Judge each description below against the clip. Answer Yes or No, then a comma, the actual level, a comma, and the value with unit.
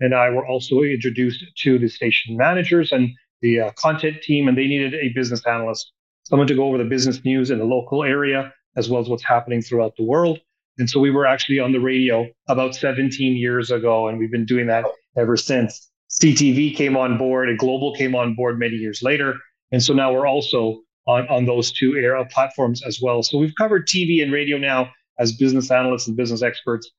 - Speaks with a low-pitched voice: Yes, low, 130 Hz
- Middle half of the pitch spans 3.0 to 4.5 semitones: No, narrow, 2.4 semitones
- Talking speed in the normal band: No, fast, 215 wpm